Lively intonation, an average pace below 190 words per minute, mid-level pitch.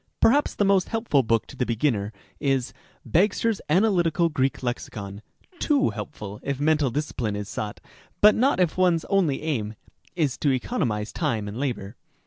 Yes: wide, 8.0 semitones; average, 165 wpm; medium, 145 Hz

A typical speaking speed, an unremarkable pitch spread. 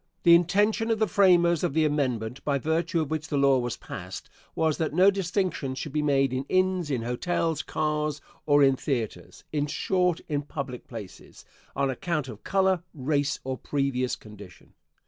Yes: average, 175 wpm; average, 4.5 semitones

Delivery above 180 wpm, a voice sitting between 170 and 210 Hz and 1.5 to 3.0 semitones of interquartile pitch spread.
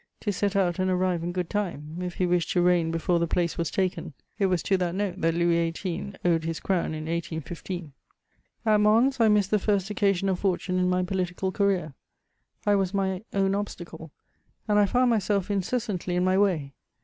Yes: average, 200 wpm; medium, 185 Hz; average, 2.7 semitones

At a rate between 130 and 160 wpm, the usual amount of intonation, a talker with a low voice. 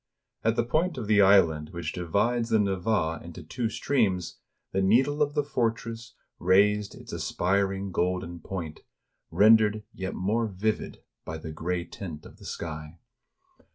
Yes: average, 150 wpm; average, 4.6 semitones; low, 100 Hz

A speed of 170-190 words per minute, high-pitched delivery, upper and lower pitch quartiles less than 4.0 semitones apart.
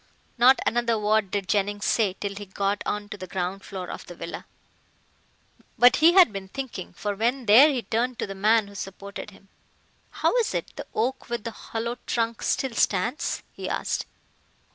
Yes: average, 185 wpm; high, 215 Hz; average, 3.4 semitones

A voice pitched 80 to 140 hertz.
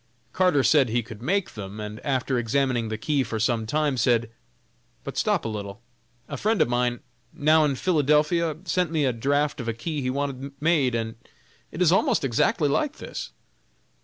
Yes: low, 135 Hz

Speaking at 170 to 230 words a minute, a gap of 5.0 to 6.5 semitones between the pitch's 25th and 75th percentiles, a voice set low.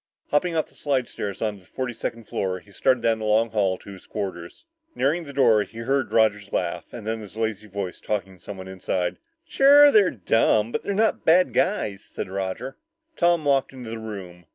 Yes: average, 200 wpm; wide, 5.5 semitones; low, 110 Hz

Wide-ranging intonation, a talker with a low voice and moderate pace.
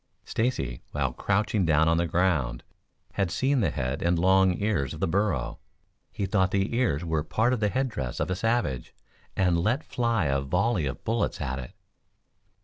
Yes: wide, 6.5 semitones; very low, 90 Hz; average, 185 wpm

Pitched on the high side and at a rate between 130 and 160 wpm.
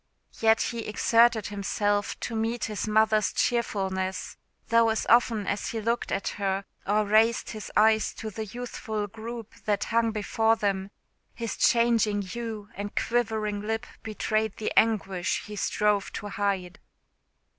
Yes: high, 215 Hz; average, 145 wpm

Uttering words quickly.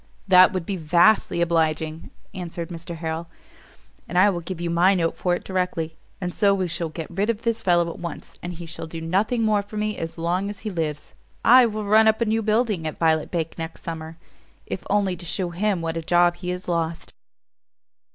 Yes: fast, 215 wpm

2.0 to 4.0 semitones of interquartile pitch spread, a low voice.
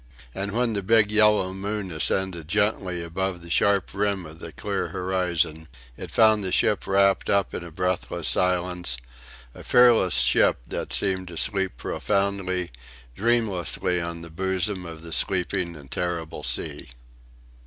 Yes: average, 2.8 semitones; very low, 95 Hz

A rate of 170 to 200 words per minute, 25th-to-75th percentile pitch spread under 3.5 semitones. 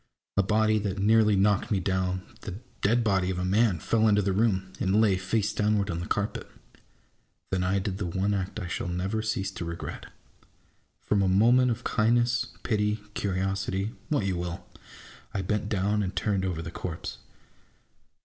Yes: average, 180 wpm; narrow, 2.4 semitones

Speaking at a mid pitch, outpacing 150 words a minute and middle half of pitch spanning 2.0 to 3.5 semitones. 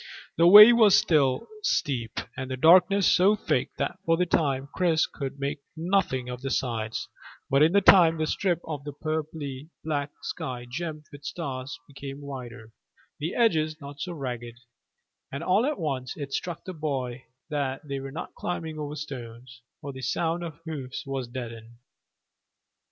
No: medium, 145 Hz; average, 170 wpm; average, 4.0 semitones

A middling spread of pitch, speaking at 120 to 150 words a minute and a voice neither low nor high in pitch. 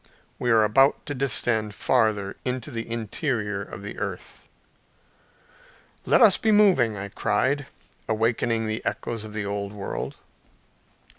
No: average, 3.5 semitones; slow, 135 wpm; low, 115 Hz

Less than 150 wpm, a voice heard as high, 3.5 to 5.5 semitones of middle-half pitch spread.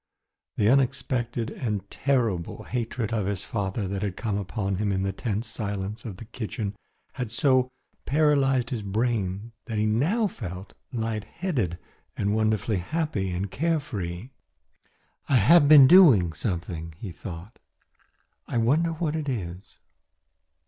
No: average, 140 wpm; low, 110 Hz; average, 5.1 semitones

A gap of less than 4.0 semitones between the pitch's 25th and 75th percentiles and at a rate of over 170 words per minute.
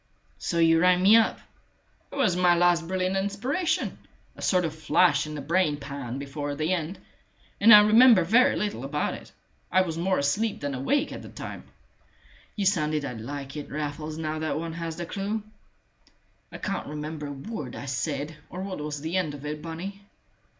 No: average, 4.3 semitones; average, 185 wpm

